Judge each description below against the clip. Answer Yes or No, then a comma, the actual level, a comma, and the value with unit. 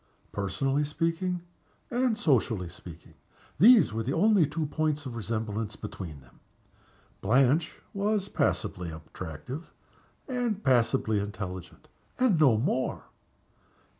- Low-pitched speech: Yes, low, 130 Hz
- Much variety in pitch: Yes, wide, 8.6 semitones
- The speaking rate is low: Yes, slow, 105 wpm